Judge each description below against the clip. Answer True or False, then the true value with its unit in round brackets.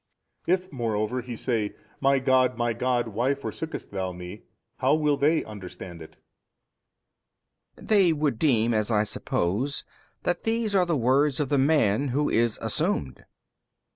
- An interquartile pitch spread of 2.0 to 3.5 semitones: False (5.4 semitones)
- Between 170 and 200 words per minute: False (155 wpm)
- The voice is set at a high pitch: False (125 Hz)